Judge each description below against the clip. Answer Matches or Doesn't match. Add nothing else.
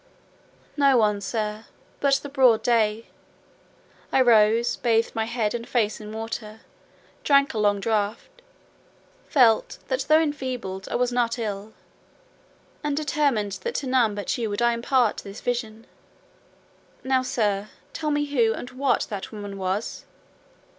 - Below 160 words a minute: Matches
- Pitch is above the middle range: Matches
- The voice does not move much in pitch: Doesn't match